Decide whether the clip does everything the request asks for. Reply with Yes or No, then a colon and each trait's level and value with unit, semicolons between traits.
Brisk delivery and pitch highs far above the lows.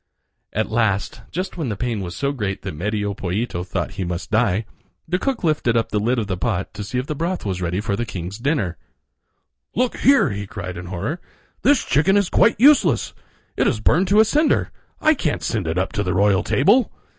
Yes: fast, 215 wpm; wide, 8.9 semitones